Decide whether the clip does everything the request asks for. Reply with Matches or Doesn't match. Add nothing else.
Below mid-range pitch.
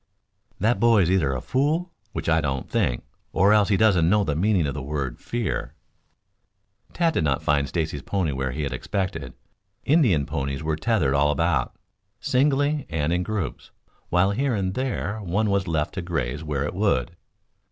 Matches